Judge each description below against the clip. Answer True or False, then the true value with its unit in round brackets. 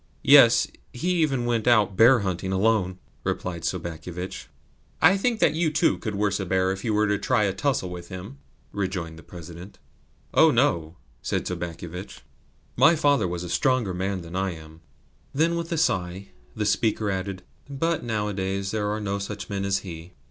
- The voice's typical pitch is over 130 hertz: False (100 Hz)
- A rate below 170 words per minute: False (180 wpm)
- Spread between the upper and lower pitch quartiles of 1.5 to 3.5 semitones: False (4.7 semitones)